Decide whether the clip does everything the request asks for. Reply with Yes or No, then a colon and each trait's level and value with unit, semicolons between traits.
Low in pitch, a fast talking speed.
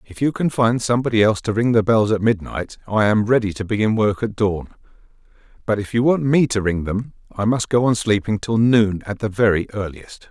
Yes: low, 110 Hz; fast, 225 wpm